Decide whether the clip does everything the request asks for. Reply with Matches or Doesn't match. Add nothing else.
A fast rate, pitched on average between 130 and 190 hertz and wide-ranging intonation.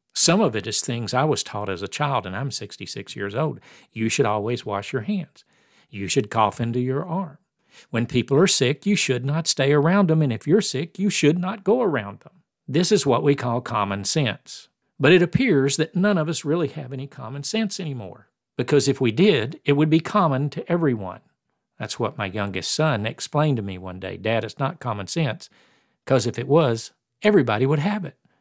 Matches